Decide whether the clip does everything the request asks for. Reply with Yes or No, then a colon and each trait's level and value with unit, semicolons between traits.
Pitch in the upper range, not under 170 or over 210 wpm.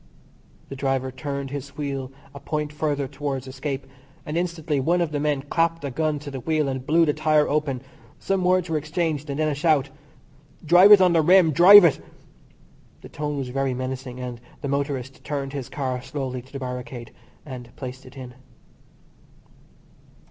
No: medium, 140 Hz; average, 180 wpm